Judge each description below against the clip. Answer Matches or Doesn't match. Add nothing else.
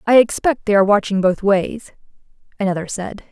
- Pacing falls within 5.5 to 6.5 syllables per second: Matches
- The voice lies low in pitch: Doesn't match